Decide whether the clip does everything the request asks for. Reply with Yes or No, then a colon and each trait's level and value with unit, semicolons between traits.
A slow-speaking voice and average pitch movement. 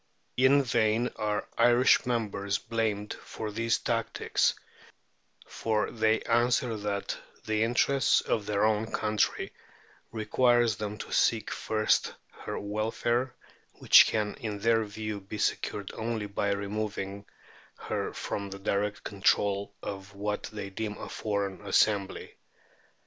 No: slow, 125 wpm; narrow, 2.1 semitones